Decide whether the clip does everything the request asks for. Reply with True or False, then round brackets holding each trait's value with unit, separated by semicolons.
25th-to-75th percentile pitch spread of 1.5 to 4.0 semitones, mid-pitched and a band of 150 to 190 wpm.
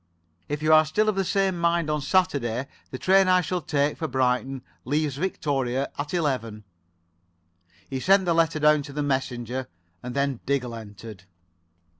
False (4.7 semitones; 145 Hz; 165 wpm)